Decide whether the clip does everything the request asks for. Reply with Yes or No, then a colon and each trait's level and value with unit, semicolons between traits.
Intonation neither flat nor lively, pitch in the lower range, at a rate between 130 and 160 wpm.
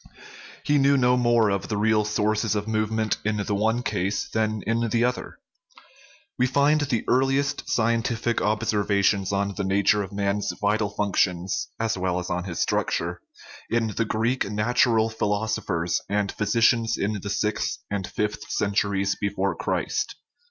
No: narrow, 2.3 semitones; low, 105 Hz; average, 155 wpm